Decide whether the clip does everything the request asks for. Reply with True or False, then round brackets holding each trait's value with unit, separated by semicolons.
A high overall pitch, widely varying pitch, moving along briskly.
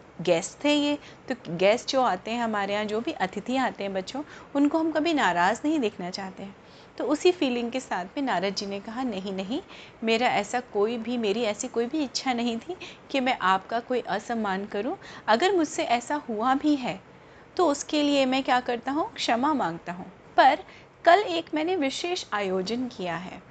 True (245 Hz; 6.5 semitones; 195 wpm)